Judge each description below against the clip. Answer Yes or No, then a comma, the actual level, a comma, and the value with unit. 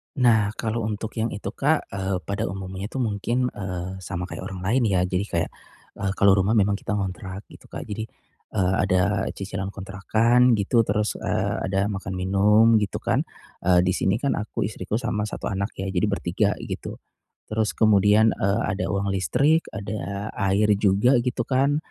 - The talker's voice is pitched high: No, low, 100 Hz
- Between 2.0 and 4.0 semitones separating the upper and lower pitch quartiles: Yes, narrow, 2.4 semitones